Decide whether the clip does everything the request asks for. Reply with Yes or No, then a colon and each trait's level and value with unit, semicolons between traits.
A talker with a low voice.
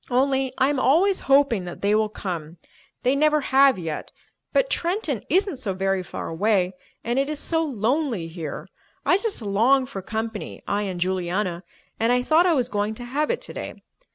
No: high, 240 Hz